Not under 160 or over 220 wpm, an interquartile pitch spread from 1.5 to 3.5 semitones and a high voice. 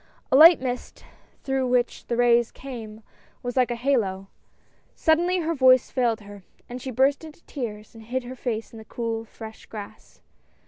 Yes: average, 175 wpm; average, 2.9 semitones; high, 245 Hz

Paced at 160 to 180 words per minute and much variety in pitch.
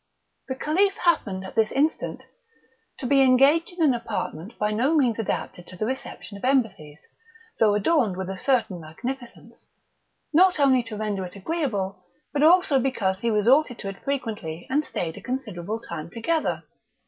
Yes: average, 165 wpm; wide, 6.2 semitones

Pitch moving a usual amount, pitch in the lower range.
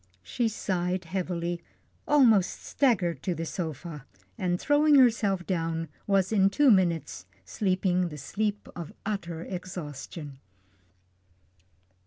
No: average, 3.5 semitones; medium, 180 Hz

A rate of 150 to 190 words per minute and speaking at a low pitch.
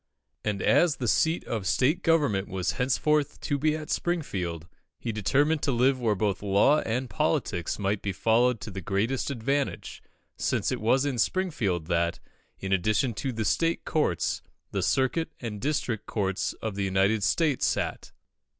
Yes: average, 165 wpm; low, 115 Hz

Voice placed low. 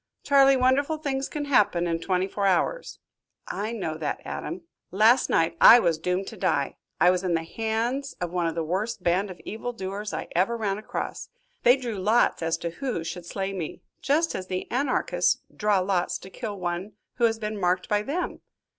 No: high, 200 Hz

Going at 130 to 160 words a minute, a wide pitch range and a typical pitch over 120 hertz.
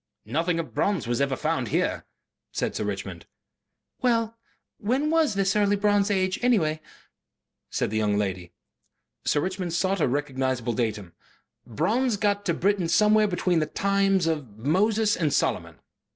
Yes: average, 150 wpm; wide, 6.5 semitones; medium, 185 Hz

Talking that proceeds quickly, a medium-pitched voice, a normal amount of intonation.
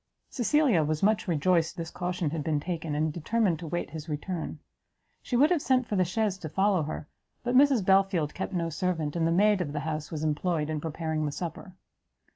Yes: fast, 210 wpm; medium, 170 Hz; average, 3.9 semitones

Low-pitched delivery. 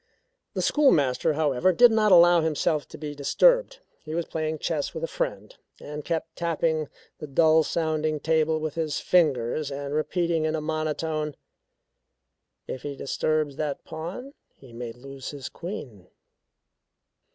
No: medium, 155 Hz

